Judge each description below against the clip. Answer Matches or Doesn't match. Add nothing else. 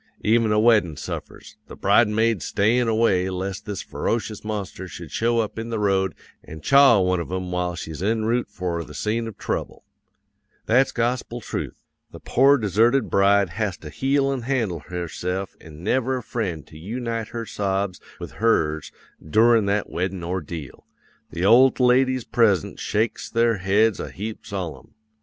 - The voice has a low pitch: Matches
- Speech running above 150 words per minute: Matches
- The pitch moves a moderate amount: Matches